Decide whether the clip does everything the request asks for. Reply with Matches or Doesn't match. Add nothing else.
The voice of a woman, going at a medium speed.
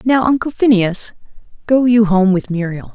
Matches